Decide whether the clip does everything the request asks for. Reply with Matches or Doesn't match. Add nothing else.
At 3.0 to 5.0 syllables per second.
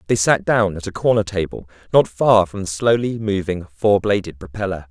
Doesn't match